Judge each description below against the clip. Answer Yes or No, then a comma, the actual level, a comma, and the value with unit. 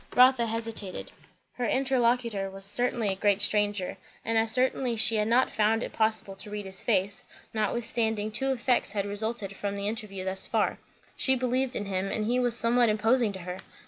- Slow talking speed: No, average, 185 wpm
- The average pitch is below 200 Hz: No, high, 220 Hz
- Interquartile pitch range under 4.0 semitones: Yes, average, 3.0 semitones